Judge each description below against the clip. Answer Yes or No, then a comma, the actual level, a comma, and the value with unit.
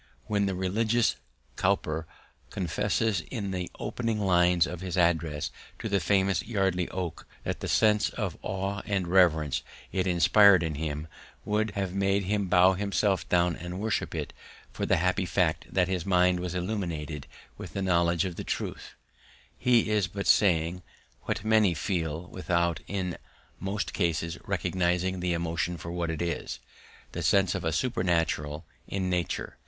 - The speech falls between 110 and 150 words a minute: No, average, 160 wpm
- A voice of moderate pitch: No, very low, 90 Hz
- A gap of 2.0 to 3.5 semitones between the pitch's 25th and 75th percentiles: Yes, average, 2.7 semitones